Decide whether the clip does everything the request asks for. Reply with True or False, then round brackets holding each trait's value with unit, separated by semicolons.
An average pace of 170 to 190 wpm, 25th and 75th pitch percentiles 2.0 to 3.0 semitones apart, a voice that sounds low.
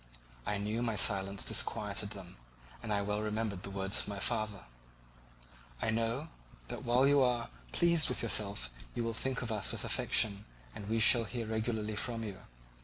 True (180 wpm; 2.5 semitones; 110 Hz)